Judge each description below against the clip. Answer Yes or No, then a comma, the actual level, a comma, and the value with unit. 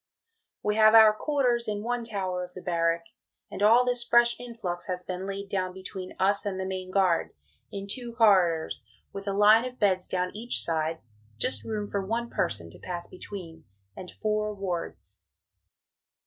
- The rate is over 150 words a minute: Yes, average, 175 wpm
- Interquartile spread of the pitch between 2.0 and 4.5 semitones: Yes, average, 3.5 semitones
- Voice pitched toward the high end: Yes, high, 200 Hz